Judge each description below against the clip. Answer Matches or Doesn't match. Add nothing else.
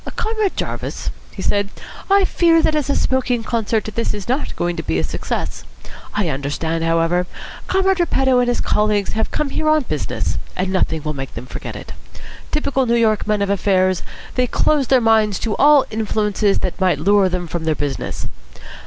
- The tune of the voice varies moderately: Doesn't match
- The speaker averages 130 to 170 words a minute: Doesn't match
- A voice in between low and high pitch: Doesn't match